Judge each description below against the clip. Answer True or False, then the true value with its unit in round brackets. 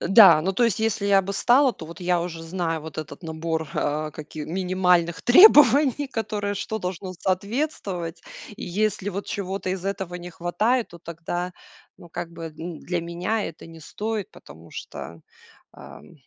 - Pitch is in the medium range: True (180 Hz)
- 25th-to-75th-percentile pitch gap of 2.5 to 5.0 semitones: True (3.7 semitones)